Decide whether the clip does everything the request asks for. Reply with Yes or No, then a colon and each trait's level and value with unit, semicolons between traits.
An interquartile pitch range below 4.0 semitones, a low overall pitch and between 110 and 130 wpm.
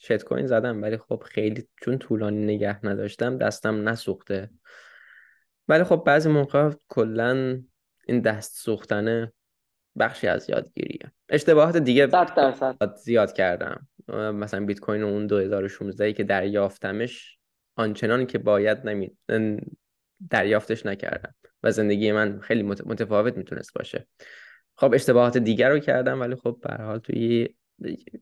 Yes: average, 2.8 semitones; low, 110 Hz; average, 125 wpm